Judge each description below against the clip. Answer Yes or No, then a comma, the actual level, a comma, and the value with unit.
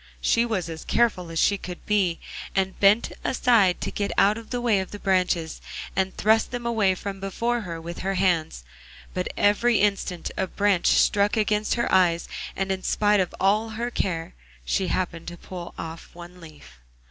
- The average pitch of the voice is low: No, high, 195 Hz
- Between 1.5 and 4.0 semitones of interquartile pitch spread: Yes, average, 3.1 semitones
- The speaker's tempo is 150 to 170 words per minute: No, average, 185 wpm